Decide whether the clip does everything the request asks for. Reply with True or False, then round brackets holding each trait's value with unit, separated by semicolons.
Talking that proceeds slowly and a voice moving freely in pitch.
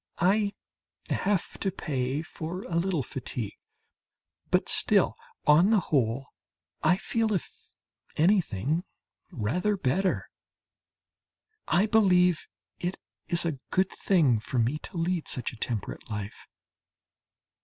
True (115 wpm; 6.6 semitones)